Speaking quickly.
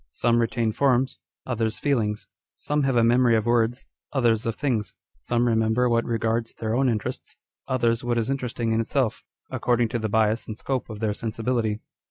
No: average, 185 wpm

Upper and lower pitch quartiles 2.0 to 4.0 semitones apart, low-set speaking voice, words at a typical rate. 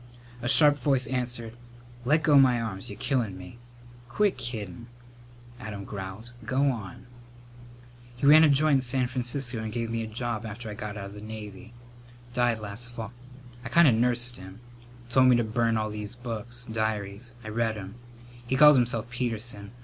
Yes: average, 2.7 semitones; low, 120 Hz; average, 175 wpm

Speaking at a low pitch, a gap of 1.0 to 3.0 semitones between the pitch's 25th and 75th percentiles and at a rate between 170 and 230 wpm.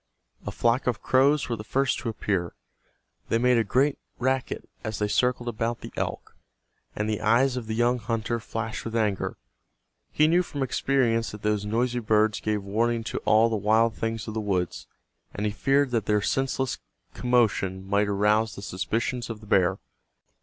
Yes: low, 115 Hz; average, 2.7 semitones; average, 180 wpm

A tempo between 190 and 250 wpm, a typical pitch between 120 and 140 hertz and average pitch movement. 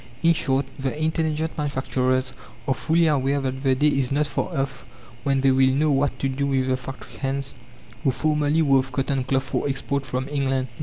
No: average, 200 wpm; low, 135 Hz; narrow, 1.8 semitones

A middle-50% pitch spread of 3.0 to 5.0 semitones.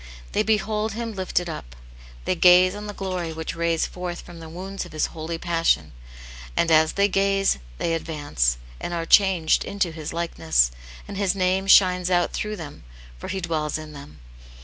Yes: average, 3.3 semitones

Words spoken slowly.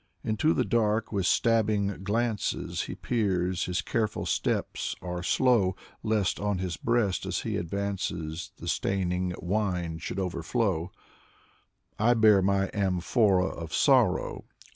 Yes: slow, 125 wpm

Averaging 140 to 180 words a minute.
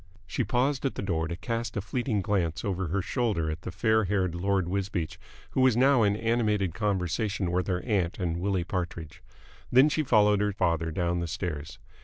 No: average, 195 wpm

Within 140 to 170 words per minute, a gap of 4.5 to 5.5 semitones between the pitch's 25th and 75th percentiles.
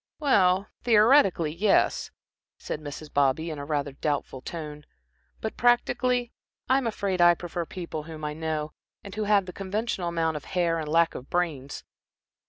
Yes: average, 160 wpm; average, 4.9 semitones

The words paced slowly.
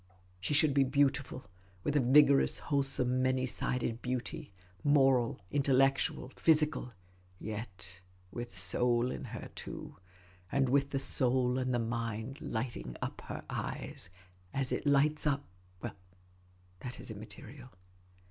Yes: slow, 130 wpm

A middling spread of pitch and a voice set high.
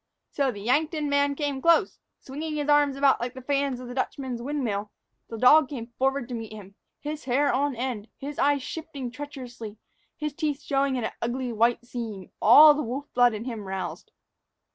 Yes: average, 3.4 semitones; very high, 265 Hz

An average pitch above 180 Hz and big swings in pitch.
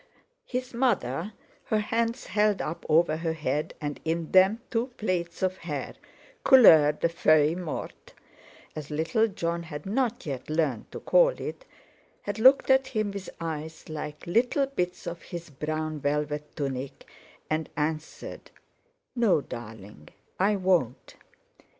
No: medium, 170 Hz; wide, 6.0 semitones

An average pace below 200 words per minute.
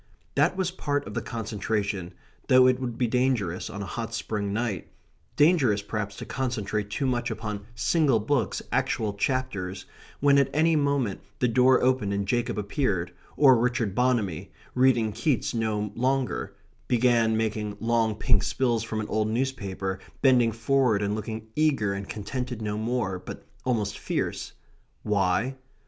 Yes: average, 155 wpm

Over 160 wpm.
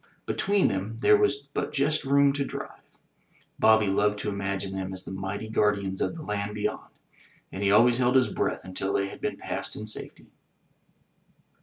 Yes: average, 180 wpm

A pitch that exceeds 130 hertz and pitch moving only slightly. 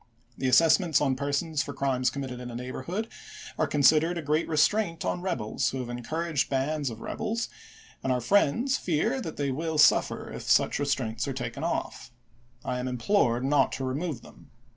No: medium, 140 Hz; average, 4.4 semitones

